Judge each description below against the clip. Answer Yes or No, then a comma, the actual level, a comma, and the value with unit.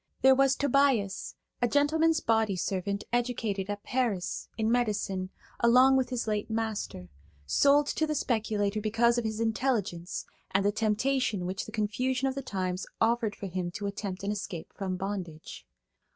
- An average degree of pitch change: Yes, average, 4.2 semitones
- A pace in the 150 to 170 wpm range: Yes, average, 160 wpm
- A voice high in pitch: Yes, high, 220 Hz